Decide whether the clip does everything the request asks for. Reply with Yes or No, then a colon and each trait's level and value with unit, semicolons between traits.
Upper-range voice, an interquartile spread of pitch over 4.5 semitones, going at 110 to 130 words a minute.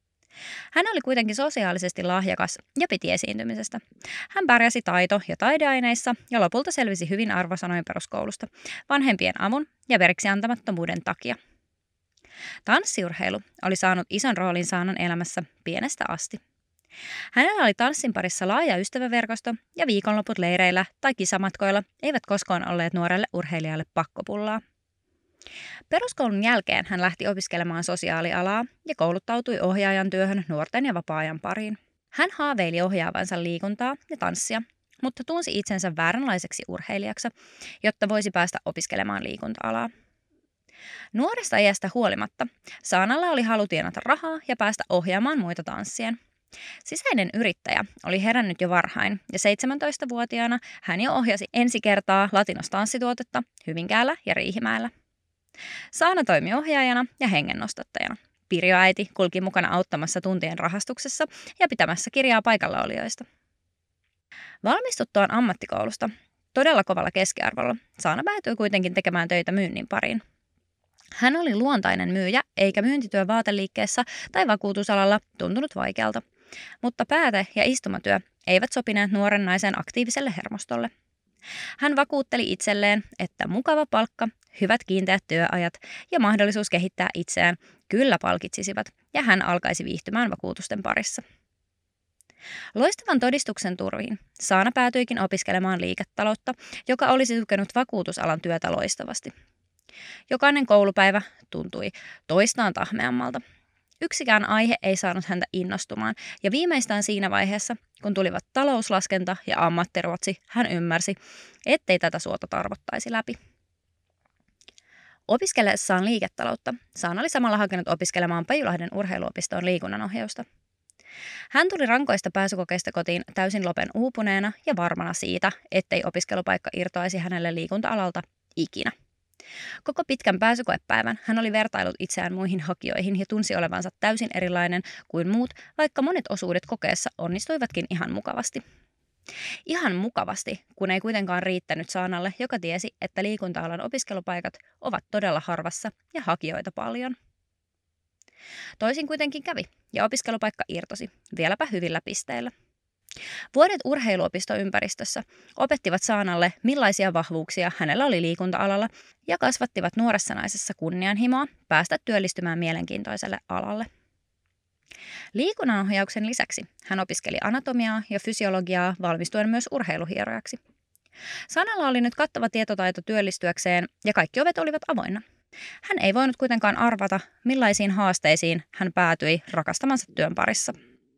Yes: high, 200 Hz; average, 5.0 semitones; average, 115 wpm